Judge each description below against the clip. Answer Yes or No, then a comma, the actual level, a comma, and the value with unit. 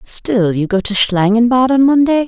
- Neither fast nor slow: Yes, average, 185 wpm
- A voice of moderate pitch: No, high, 230 Hz